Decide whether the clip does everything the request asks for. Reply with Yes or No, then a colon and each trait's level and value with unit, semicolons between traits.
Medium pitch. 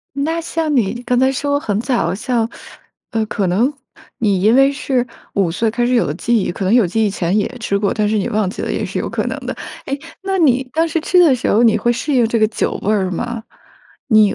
No: high, 230 Hz